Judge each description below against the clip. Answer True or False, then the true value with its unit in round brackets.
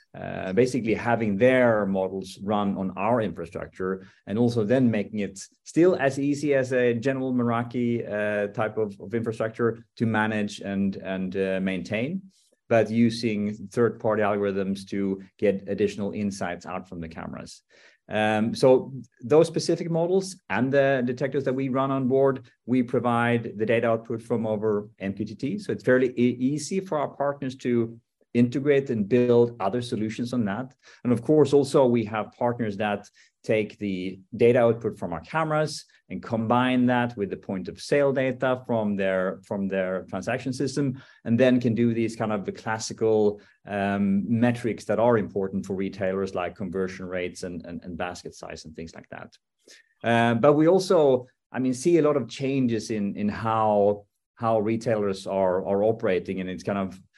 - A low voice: True (115 Hz)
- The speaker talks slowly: False (170 wpm)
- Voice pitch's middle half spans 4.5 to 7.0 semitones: False (4.0 semitones)